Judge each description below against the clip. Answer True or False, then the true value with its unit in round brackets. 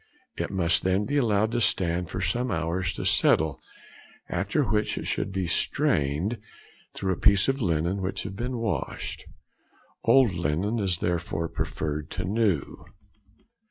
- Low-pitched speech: True (95 Hz)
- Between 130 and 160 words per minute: True (150 wpm)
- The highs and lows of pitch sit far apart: False (4.2 semitones)